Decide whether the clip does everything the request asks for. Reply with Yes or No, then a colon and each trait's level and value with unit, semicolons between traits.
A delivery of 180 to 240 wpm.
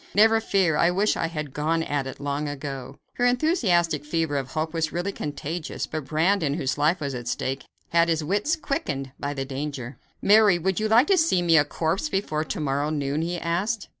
Yes: fast, 205 wpm